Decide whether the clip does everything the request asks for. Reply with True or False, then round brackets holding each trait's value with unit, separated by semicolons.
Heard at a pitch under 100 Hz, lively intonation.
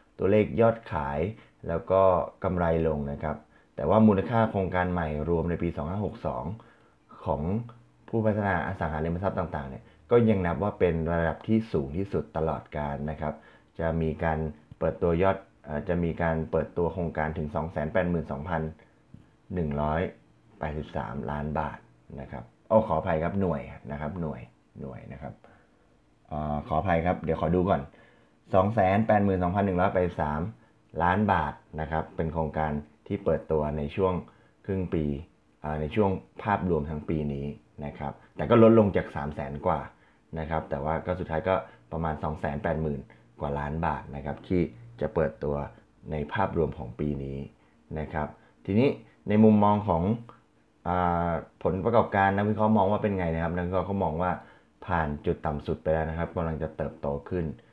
False (80 Hz; 3.9 semitones)